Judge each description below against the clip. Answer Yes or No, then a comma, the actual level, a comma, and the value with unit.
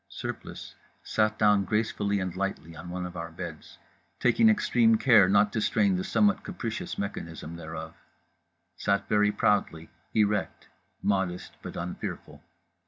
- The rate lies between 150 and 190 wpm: No, slow, 135 wpm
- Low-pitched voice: Yes, low, 100 Hz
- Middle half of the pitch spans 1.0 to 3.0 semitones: No, average, 3.7 semitones